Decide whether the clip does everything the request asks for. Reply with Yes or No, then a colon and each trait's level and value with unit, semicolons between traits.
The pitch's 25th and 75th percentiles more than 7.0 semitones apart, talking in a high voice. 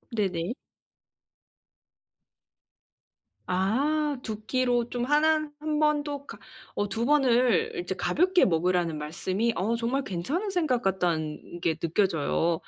Yes: wide, 8.4 semitones; high, 235 Hz